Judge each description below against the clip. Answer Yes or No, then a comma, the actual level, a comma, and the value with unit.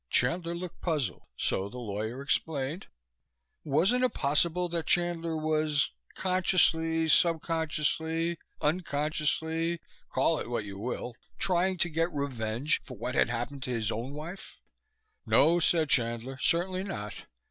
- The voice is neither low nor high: Yes, medium, 155 Hz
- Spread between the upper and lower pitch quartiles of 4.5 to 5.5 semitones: Yes, average, 5.0 semitones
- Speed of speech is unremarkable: No, slow, 130 wpm